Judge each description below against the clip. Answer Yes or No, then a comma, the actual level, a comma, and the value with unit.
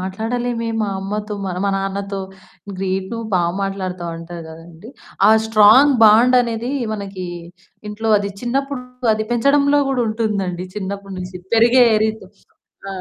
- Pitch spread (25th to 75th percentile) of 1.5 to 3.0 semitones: No, average, 3.5 semitones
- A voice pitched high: Yes, high, 210 Hz